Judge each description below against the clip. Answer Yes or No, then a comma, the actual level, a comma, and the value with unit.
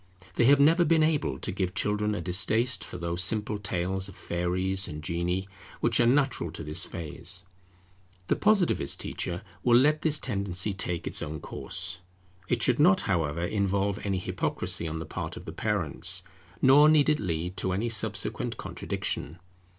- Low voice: Yes, very low, 95 Hz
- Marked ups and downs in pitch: Yes, wide, 5.9 semitones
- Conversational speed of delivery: Yes, average, 170 wpm